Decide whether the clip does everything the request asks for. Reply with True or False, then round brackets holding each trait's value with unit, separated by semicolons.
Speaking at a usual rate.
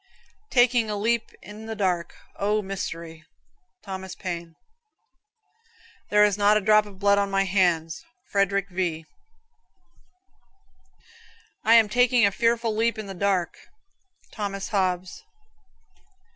False (120 wpm)